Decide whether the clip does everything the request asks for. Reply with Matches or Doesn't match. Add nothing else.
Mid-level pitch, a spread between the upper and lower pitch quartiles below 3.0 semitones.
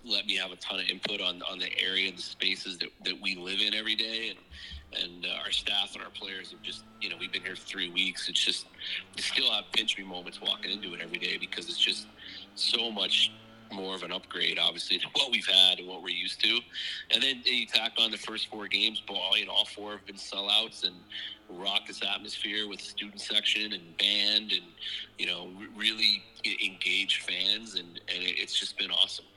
Doesn't match